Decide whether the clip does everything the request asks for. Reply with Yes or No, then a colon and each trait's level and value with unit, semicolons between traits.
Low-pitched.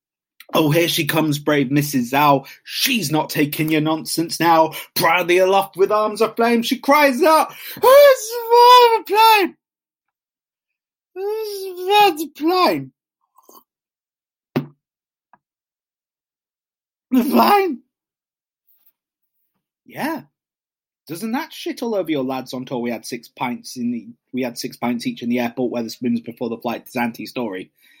No: high, 190 Hz